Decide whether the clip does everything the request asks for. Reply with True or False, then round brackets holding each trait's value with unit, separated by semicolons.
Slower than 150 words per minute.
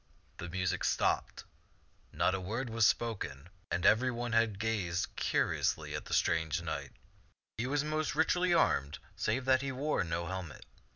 False (155 wpm)